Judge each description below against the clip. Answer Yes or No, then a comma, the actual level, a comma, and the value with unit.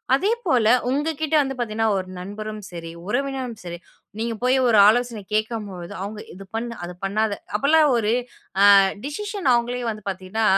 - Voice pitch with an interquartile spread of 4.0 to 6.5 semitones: Yes, average, 4.3 semitones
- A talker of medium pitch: No, high, 225 Hz